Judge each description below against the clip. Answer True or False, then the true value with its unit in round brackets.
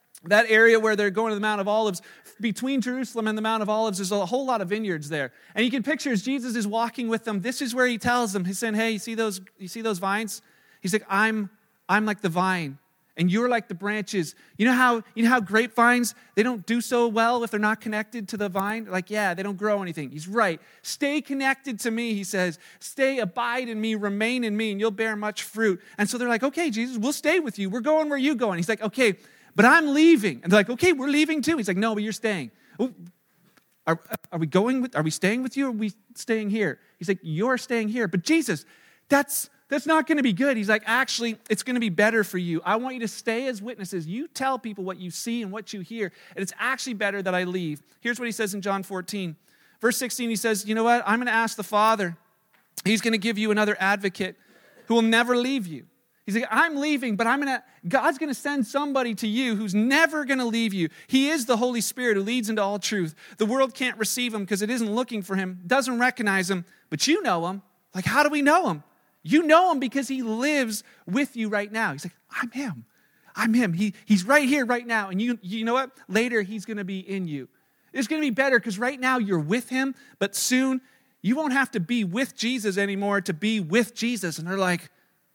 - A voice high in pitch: True (225 Hz)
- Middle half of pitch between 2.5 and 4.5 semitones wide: True (3.8 semitones)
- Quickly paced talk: True (245 wpm)